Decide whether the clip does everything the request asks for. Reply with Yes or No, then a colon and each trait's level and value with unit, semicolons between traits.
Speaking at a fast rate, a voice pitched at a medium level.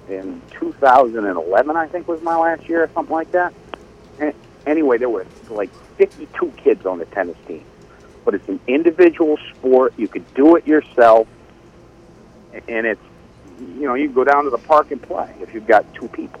No: average, 185 wpm; medium, 165 Hz